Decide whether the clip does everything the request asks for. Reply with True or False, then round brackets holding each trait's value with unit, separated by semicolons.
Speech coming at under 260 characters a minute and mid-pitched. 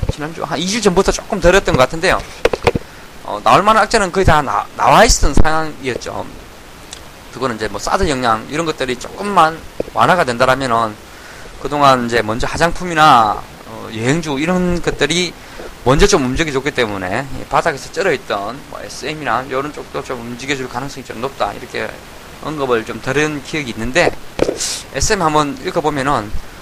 False (335 characters per minute; 145 Hz)